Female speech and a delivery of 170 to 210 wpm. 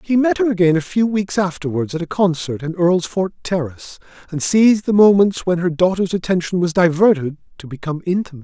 No: male; average, 190 wpm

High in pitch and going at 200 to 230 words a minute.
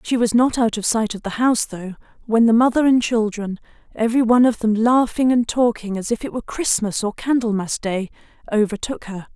Yes: high, 225 Hz; fast, 205 wpm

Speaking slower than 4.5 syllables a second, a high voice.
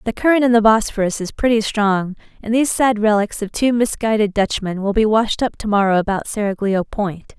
No: 5.4 syllables/s; high, 215 Hz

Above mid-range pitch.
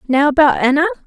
Yes: very high, 300 Hz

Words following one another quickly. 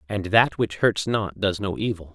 Yes: fast, 225 wpm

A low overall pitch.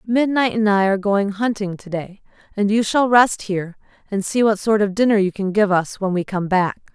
No: high, 205 Hz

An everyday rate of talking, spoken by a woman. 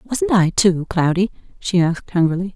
Yes: average, 165 wpm; female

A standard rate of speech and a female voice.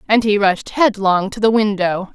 Yes: average, 195 wpm; female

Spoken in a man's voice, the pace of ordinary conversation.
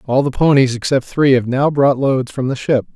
No: male; fast, 245 wpm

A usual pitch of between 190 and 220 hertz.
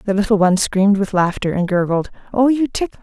Yes: high, 200 Hz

